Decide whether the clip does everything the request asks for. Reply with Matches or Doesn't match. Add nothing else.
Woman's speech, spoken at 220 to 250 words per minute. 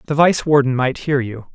Doesn't match